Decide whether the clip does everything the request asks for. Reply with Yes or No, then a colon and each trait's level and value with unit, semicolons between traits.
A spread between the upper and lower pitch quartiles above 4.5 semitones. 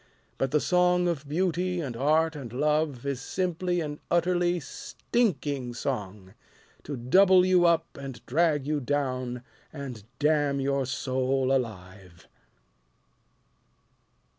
Yes: average, 5.0 semitones